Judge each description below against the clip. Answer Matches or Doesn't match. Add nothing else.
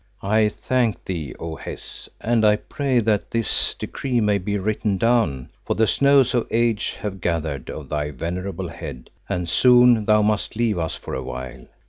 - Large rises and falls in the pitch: Matches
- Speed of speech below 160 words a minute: Doesn't match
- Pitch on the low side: Matches